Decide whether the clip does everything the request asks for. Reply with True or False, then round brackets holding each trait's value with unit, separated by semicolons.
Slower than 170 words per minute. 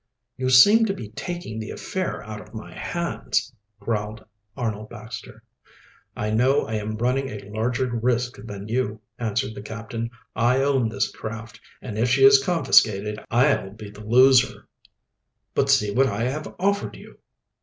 True (160 wpm)